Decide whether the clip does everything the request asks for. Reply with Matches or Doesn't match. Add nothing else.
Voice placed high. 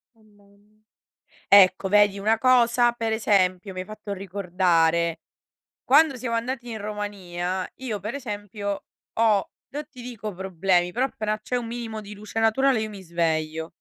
Matches